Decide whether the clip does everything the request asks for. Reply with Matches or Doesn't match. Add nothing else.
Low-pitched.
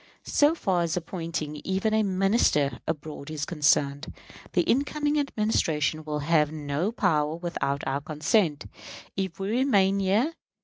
Doesn't match